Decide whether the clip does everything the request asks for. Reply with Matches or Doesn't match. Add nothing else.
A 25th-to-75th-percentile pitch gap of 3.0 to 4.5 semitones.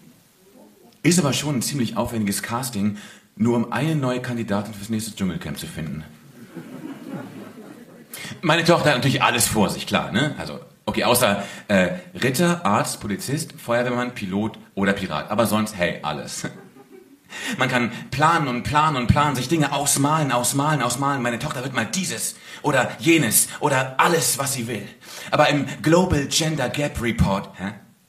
Matches